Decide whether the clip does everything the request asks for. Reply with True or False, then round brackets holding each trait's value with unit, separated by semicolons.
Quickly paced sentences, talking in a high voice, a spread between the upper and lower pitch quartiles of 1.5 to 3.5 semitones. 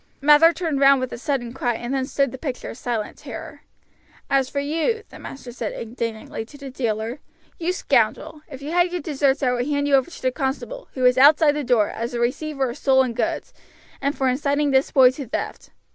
True (220 wpm; 270 Hz; 2.9 semitones)